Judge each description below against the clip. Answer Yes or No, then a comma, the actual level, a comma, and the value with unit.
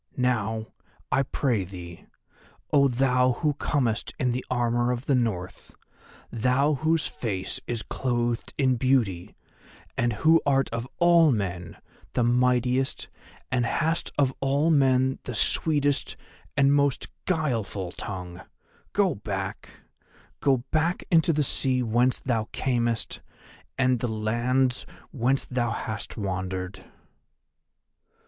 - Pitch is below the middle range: Yes, low, 125 Hz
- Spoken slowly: Yes, slow, 120 wpm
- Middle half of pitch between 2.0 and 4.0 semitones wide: Yes, average, 3.5 semitones